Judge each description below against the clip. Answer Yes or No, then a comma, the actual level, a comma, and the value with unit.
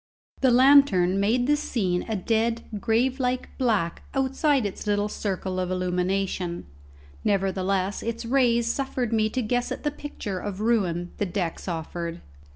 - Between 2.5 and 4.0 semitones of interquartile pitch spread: No, average, 5.0 semitones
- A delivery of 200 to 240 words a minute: No, average, 150 wpm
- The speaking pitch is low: No, high, 210 Hz